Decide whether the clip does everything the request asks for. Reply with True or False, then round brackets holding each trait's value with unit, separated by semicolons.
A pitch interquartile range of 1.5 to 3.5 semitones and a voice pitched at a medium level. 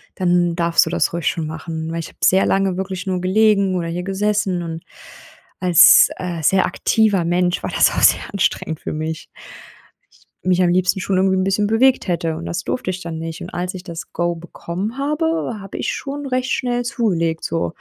True (2.9 semitones; 180 Hz)